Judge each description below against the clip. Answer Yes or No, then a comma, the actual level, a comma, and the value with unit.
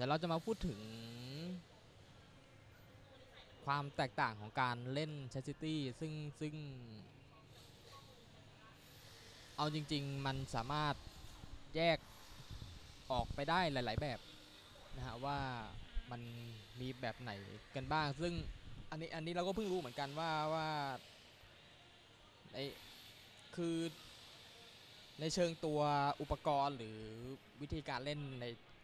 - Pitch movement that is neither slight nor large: Yes, average, 4.8 semitones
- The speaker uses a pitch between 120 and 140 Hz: Yes, low, 135 Hz